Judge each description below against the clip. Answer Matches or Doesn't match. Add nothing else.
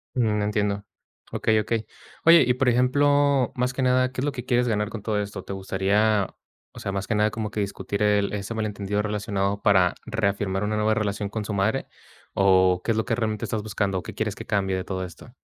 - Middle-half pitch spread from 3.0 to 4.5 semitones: Doesn't match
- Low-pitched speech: Matches